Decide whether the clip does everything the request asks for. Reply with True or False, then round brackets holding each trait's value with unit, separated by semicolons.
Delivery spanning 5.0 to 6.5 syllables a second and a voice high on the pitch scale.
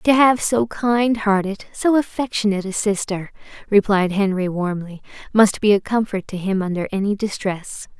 False (4.8 syllables/s; 205 Hz)